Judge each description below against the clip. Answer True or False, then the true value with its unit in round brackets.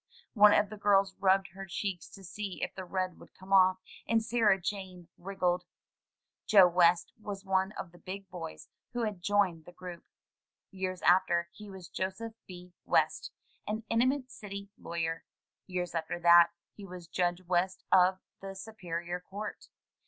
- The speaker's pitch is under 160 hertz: False (190 Hz)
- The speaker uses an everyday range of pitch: False (2.1 semitones)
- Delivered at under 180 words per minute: True (160 wpm)